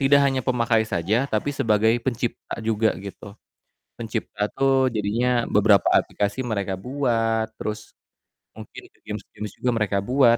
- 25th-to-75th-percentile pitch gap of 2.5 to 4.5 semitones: Yes, average, 3.0 semitones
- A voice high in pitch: No, low, 110 Hz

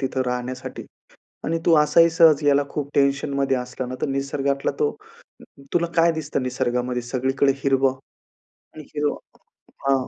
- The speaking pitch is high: No, medium, 140 Hz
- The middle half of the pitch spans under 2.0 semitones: No, narrow, 2.6 semitones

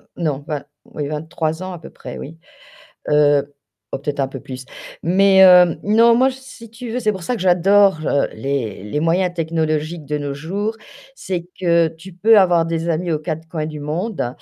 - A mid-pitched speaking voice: Yes, medium, 165 Hz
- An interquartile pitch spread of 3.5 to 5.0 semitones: Yes, average, 4.1 semitones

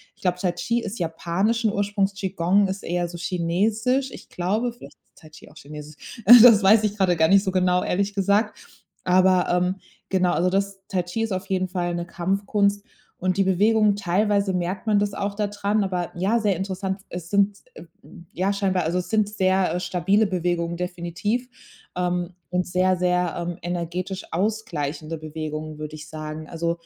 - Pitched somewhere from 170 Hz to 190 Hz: Yes, medium, 185 Hz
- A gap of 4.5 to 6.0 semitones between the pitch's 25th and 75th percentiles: No, narrow, 2.6 semitones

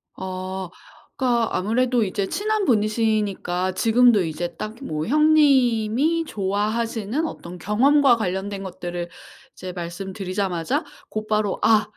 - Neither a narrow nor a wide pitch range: Yes, average, 4.5 semitones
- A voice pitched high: Yes, high, 210 Hz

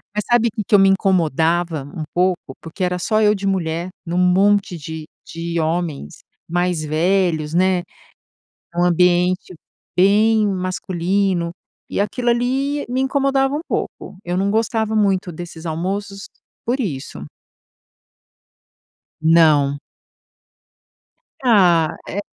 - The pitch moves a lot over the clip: No, average, 3.7 semitones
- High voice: No, medium, 180 Hz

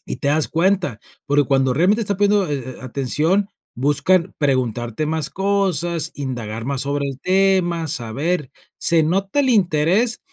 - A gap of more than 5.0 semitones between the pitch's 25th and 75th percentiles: Yes, wide, 5.6 semitones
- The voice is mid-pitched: Yes, medium, 160 Hz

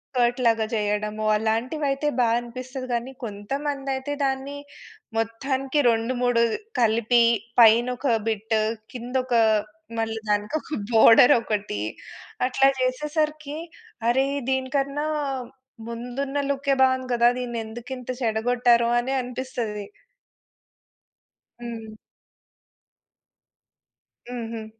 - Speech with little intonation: No, average, 3.0 semitones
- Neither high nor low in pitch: No, high, 245 Hz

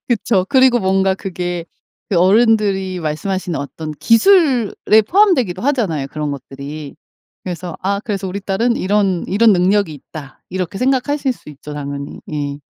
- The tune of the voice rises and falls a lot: Yes, wide, 6.3 semitones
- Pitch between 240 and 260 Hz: No, high, 190 Hz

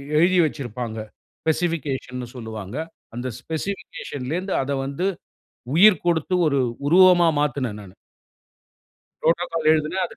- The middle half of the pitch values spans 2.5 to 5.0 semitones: No, wide, 5.5 semitones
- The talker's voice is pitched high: No, medium, 150 Hz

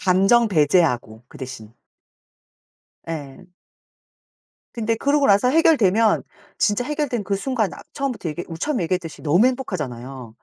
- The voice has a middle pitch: No, high, 195 Hz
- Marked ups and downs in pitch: Yes, wide, 8.2 semitones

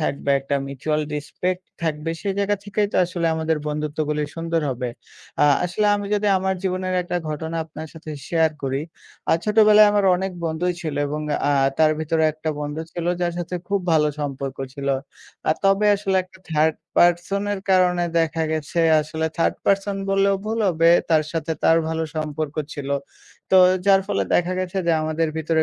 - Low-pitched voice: No, medium, 165 Hz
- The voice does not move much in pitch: No, average, 3.5 semitones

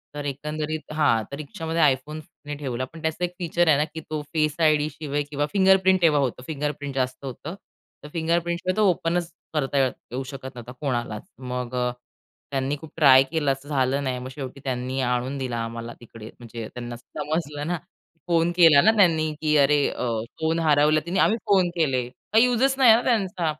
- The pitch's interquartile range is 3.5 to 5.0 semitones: Yes, average, 3.9 semitones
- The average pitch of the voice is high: No, medium, 150 Hz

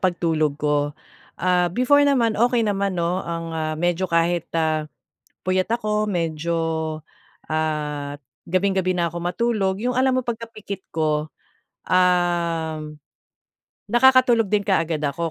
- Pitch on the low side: No, medium, 175 Hz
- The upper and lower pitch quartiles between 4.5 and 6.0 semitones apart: Yes, average, 4.9 semitones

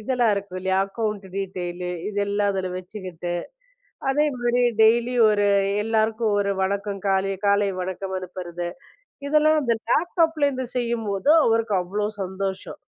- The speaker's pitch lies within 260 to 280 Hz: No, high, 205 Hz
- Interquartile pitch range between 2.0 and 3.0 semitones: No, average, 3.7 semitones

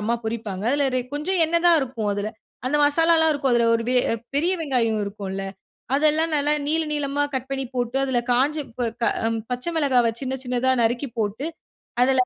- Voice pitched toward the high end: Yes, very high, 265 Hz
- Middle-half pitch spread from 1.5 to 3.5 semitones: No, average, 4.0 semitones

